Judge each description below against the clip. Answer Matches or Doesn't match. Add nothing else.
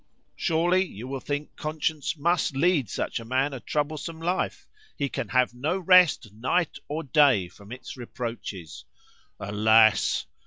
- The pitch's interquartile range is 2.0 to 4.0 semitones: Doesn't match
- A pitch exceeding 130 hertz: Matches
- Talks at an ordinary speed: Matches